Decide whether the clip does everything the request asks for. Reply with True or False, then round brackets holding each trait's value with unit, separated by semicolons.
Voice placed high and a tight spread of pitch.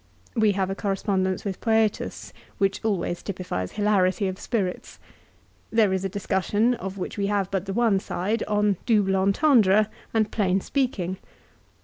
True (200 Hz; 2.2 semitones)